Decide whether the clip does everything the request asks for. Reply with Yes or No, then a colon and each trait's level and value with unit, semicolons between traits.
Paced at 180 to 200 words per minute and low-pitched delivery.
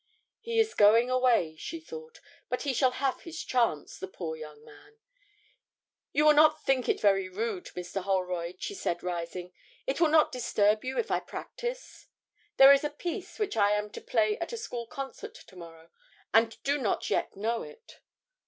No: average, 185 wpm; high, 235 Hz